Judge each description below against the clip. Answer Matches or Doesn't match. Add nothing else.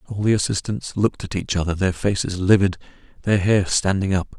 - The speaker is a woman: Doesn't match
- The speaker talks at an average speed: Matches